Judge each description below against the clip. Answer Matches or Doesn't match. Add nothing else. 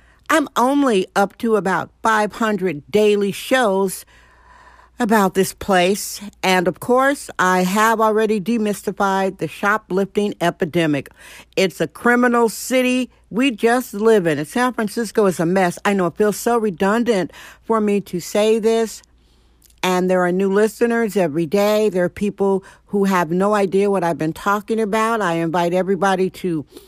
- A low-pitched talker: Doesn't match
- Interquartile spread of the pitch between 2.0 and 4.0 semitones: Matches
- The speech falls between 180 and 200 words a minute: Doesn't match